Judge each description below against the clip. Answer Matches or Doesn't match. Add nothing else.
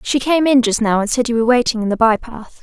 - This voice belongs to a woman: Matches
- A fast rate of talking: Matches